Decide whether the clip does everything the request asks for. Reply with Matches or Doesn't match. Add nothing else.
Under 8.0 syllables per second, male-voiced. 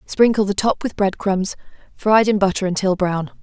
Doesn't match